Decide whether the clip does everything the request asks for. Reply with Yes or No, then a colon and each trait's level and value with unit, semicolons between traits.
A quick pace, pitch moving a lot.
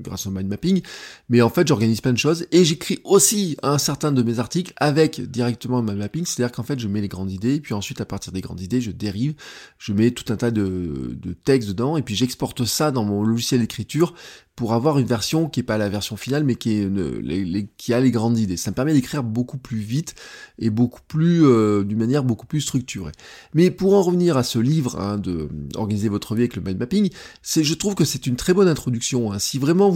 Yes: fast, 255 wpm; wide, 5.8 semitones